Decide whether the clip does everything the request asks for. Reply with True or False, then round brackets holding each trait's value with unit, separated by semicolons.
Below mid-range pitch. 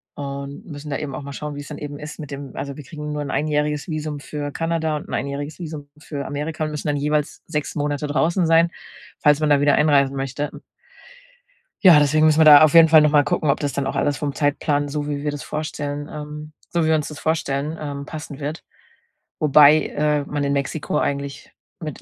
False (150 Hz)